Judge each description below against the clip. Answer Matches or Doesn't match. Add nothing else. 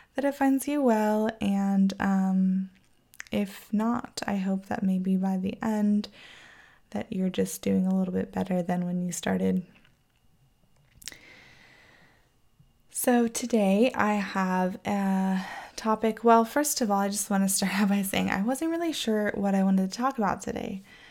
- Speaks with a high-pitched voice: Matches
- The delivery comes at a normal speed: Matches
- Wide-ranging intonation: Doesn't match